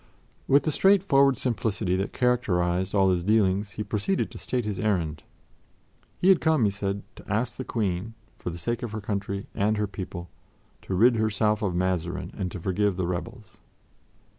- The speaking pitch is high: No, low, 105 Hz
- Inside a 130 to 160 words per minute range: No, average, 180 wpm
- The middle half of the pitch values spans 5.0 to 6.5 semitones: No, average, 3.7 semitones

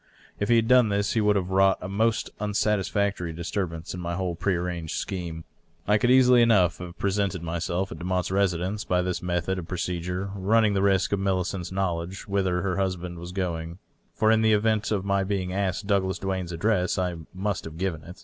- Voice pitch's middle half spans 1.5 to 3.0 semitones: Yes, narrow, 2.4 semitones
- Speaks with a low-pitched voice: Yes, very low, 95 Hz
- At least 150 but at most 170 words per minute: No, average, 200 wpm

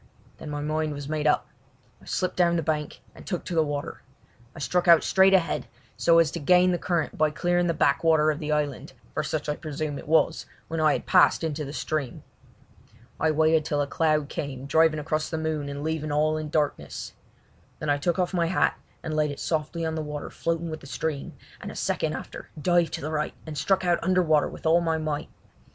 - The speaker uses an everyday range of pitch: No, narrow, 2.0 semitones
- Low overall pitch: No, medium, 155 Hz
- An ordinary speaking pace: No, fast, 225 wpm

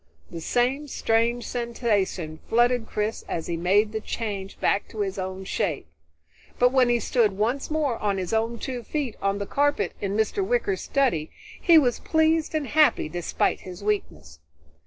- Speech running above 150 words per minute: Yes, average, 170 wpm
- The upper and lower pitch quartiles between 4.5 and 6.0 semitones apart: Yes, average, 5.0 semitones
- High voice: Yes, high, 225 Hz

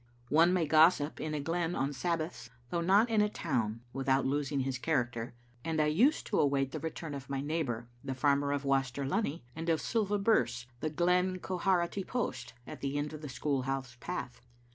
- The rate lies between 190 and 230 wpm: Yes, average, 195 wpm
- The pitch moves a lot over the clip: No, average, 4.2 semitones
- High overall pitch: No, medium, 145 Hz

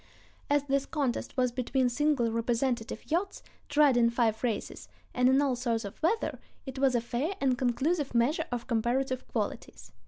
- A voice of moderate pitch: No, very high, 255 Hz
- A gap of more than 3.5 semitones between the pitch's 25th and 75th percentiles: No, average, 2.8 semitones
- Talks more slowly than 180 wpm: Yes, average, 165 wpm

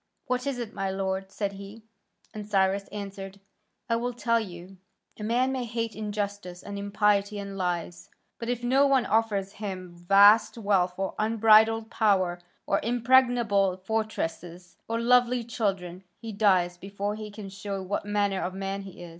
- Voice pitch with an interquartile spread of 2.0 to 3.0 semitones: Yes, average, 2.7 semitones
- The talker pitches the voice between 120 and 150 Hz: No, high, 205 Hz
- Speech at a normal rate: Yes, average, 165 wpm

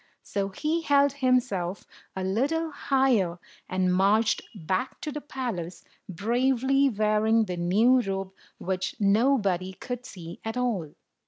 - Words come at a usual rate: No, slow, 130 wpm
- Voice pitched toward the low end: No, high, 215 Hz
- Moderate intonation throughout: No, wide, 5.7 semitones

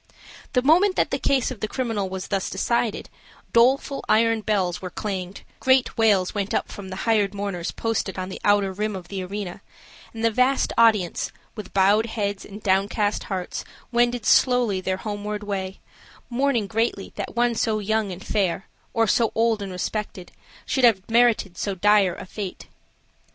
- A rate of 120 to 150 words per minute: No, average, 170 wpm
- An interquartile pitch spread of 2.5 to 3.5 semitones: Yes, average, 3.1 semitones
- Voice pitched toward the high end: Yes, high, 210 Hz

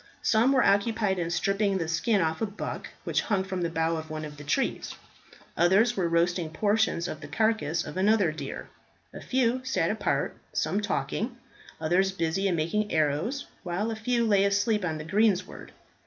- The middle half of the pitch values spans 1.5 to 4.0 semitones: No, average, 4.8 semitones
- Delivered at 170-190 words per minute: Yes, average, 185 wpm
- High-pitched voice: Yes, high, 195 Hz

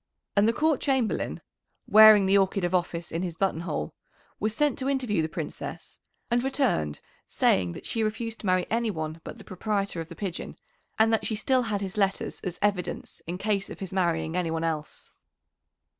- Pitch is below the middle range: No, high, 195 Hz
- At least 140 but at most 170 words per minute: No, average, 190 wpm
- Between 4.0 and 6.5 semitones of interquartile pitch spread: Yes, average, 4.6 semitones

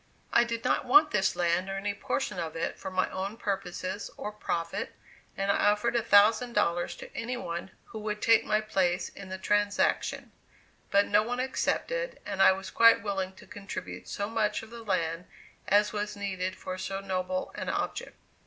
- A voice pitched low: No, high, 205 Hz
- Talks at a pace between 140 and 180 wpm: No, average, 190 wpm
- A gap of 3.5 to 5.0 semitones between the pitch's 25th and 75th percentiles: No, average, 2.8 semitones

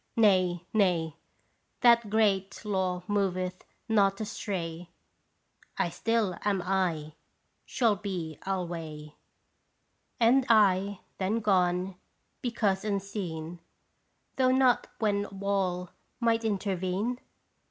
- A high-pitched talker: Yes, high, 195 Hz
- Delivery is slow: Yes, slow, 90 wpm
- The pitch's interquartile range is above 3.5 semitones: No, average, 3.0 semitones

